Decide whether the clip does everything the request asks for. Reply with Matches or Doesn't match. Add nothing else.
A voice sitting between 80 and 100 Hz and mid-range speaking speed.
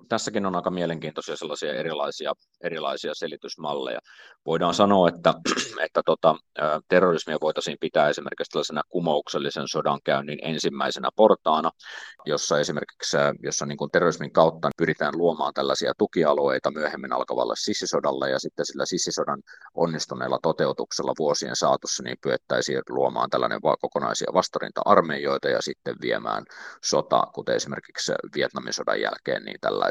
Matches